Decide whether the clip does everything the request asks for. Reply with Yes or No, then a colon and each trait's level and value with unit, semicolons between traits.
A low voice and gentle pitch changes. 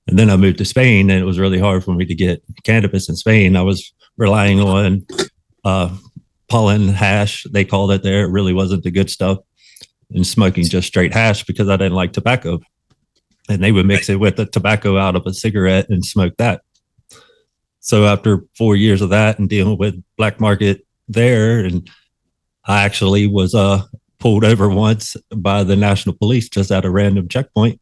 Yes: low, 100 Hz; narrow, 2.1 semitones